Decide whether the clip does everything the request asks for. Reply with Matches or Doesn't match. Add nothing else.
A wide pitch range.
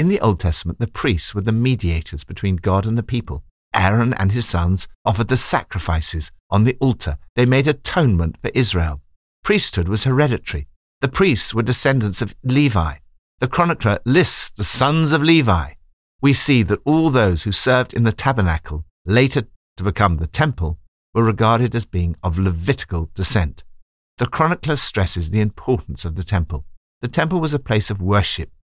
Matches